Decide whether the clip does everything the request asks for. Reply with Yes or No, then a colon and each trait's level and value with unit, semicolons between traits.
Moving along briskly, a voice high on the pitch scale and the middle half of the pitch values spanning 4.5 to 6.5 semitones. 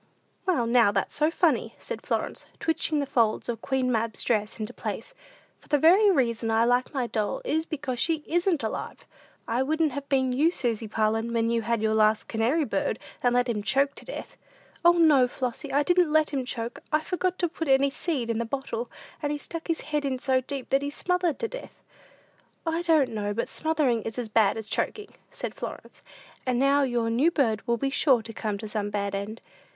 Yes: fast, 210 wpm; very high, 260 Hz; average, 5.1 semitones